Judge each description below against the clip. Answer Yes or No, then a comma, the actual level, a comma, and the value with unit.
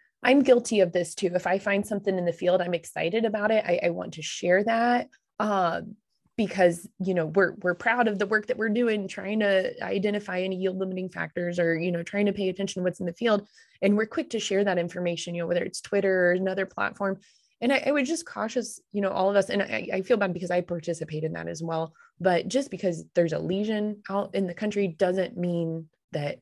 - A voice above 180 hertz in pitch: Yes, high, 190 Hz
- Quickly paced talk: Yes, fast, 240 wpm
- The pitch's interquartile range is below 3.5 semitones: Yes, average, 3.1 semitones